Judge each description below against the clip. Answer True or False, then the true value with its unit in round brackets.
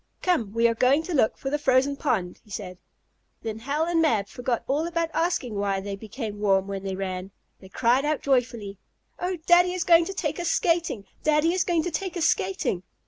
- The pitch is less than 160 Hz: False (260 Hz)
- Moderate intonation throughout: False (8.4 semitones)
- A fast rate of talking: True (210 wpm)